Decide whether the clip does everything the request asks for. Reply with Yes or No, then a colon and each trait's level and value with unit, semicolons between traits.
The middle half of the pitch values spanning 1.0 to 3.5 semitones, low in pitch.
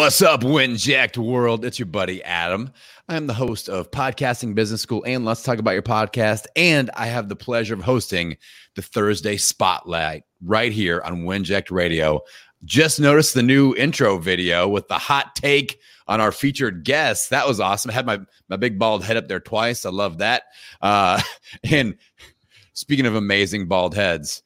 No: average, 4.3 semitones; low, 110 Hz